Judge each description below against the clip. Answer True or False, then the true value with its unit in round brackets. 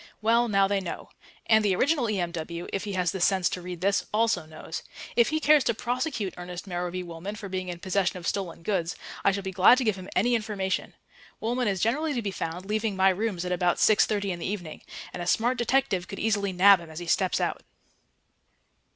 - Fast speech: True (220 wpm)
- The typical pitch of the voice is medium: False (195 Hz)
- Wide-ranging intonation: False (3.5 semitones)